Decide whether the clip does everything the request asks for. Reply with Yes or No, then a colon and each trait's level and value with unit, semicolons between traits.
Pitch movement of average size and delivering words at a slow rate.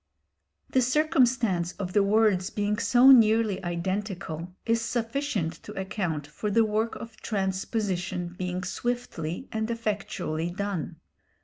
Yes: average, 4.2 semitones; slow, 120 wpm